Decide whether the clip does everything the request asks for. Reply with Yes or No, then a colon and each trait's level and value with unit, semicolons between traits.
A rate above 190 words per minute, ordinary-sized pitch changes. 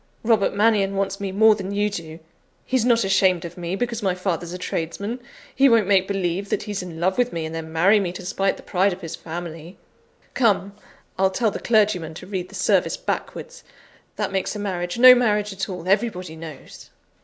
Yes: fast, 205 wpm; average, 3.1 semitones